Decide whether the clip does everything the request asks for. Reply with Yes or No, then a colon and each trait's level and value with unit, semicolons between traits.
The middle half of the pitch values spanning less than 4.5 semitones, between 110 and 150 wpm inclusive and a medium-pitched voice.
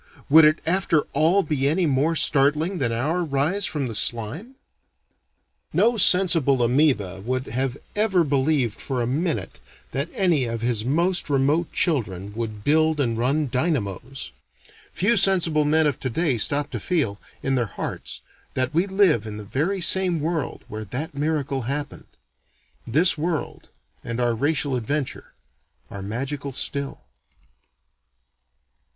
No: average, 4.9 semitones; average, 140 wpm; medium, 145 Hz